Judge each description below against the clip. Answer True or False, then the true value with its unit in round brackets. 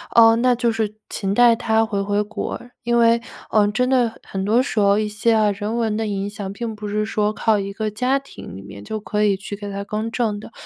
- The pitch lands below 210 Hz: False (215 Hz)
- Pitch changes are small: True (2.1 semitones)